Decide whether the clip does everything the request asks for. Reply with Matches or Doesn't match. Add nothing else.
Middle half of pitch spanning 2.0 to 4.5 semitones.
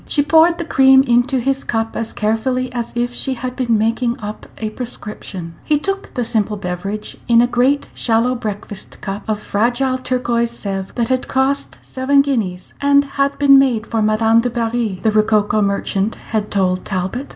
Matches